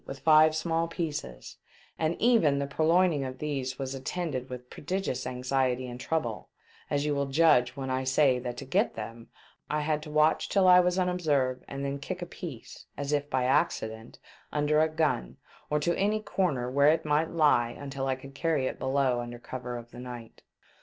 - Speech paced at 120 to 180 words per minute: No, average, 195 wpm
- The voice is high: No, medium, 140 Hz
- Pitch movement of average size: Yes, average, 3.7 semitones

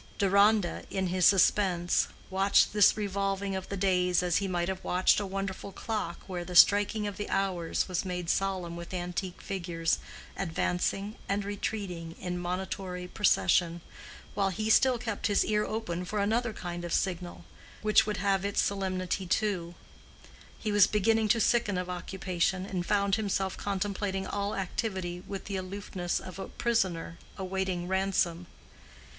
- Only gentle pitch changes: Yes, narrow, 2.2 semitones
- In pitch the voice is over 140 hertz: Yes, high, 190 Hz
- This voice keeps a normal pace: Yes, average, 155 wpm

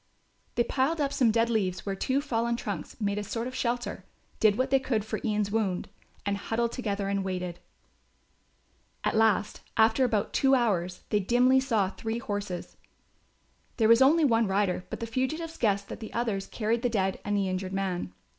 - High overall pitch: Yes, high, 220 Hz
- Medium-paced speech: Yes, average, 185 wpm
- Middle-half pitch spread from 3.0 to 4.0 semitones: Yes, average, 3.5 semitones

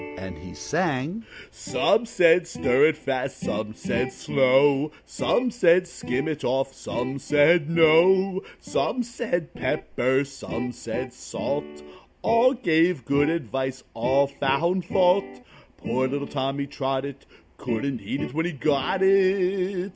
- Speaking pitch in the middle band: Yes, medium, 145 Hz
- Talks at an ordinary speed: No, slow, 130 wpm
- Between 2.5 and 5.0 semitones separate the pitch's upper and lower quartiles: No, wide, 5.4 semitones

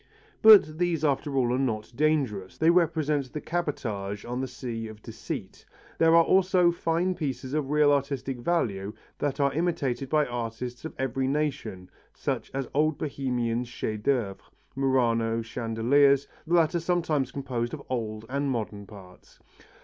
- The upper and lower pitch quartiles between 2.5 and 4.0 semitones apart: No, average, 4.7 semitones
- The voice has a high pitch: No, low, 135 Hz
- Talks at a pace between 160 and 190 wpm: No, average, 150 wpm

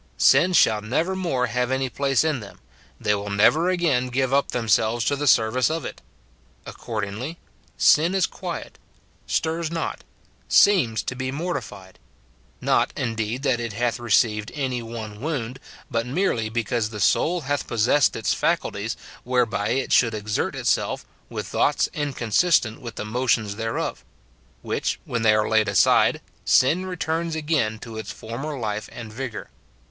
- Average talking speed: Yes, average, 155 wpm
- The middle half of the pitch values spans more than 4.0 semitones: Yes, average, 4.9 semitones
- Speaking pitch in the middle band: No, low, 125 Hz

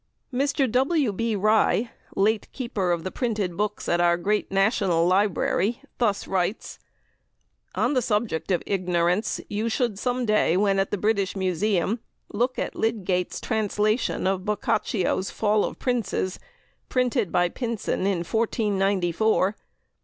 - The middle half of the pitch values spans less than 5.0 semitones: Yes, average, 3.3 semitones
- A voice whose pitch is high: Yes, high, 205 Hz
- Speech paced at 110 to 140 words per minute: Yes, slow, 135 wpm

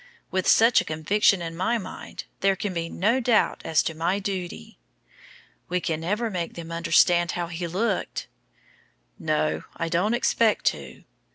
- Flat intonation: No, average, 3.7 semitones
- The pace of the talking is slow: No, average, 160 wpm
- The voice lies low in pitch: No, medium, 180 Hz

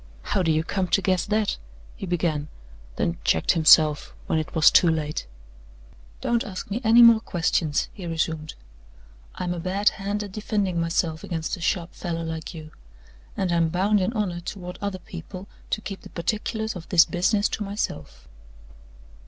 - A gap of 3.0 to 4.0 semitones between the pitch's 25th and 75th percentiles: Yes, average, 3.7 semitones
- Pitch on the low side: No, medium, 180 Hz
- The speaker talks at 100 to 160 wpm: No, average, 170 wpm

